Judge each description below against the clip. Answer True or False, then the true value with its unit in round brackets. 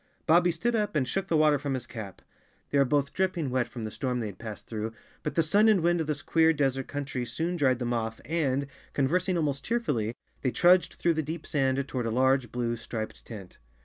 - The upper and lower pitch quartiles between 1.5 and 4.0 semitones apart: False (5.2 semitones)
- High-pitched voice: False (140 Hz)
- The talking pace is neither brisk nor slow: False (230 wpm)